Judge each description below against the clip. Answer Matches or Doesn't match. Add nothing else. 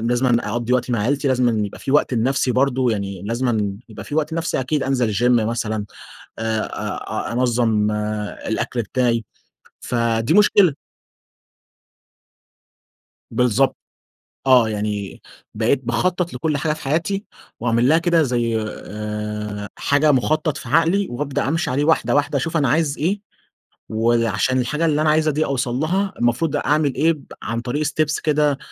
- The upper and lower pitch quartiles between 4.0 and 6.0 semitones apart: Matches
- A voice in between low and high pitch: Doesn't match